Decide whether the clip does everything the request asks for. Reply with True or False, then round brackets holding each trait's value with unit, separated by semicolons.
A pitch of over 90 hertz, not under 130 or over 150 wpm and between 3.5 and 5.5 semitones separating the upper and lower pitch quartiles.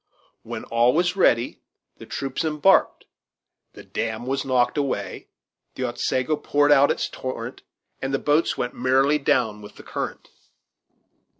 False (135 Hz; 140 wpm; 3.1 semitones)